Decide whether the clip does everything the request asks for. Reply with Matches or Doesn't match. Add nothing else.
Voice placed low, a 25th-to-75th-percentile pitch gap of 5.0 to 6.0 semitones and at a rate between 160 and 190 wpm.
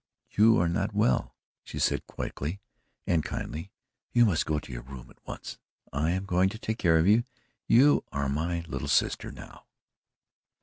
Matches